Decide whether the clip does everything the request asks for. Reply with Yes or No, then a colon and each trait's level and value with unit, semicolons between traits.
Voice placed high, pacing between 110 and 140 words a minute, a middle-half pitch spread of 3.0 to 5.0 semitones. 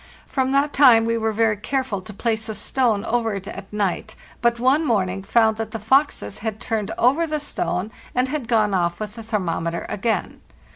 No: high, 225 Hz; average, 195 wpm; average, 3.4 semitones